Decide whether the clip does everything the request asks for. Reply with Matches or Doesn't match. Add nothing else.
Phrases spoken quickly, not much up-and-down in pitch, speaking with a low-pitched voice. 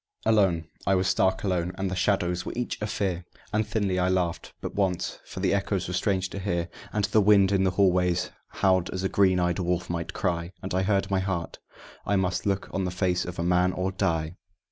Matches